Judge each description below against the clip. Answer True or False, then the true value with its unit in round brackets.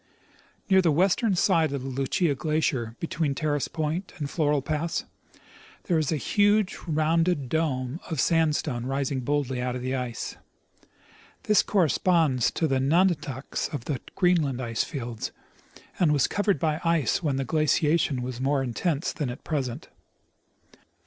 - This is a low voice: False (150 Hz)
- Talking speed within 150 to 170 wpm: True (160 wpm)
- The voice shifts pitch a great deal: False (4.1 semitones)